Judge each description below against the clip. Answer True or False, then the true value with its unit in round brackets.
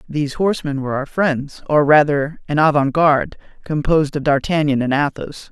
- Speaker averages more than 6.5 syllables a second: False (5.5 syllables/s)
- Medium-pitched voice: True (145 Hz)